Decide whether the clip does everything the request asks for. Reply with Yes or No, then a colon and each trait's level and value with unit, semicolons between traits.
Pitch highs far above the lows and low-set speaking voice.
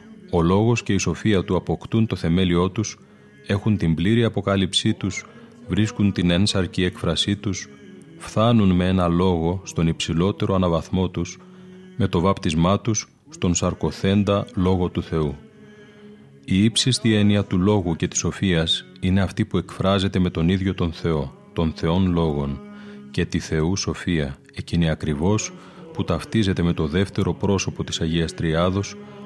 No: average, 3.4 semitones; very low, 90 Hz